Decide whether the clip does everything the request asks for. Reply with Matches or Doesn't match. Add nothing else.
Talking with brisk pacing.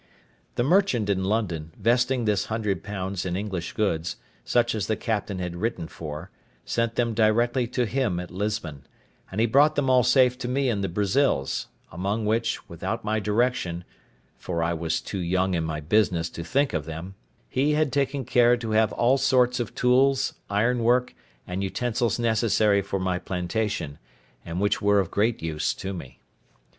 Doesn't match